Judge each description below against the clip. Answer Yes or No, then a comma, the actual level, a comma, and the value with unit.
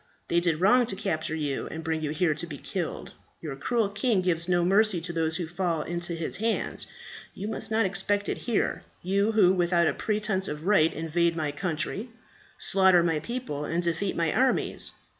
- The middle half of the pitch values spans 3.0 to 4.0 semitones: Yes, average, 3.7 semitones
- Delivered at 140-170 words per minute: No, average, 195 wpm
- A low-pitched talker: No, medium, 175 Hz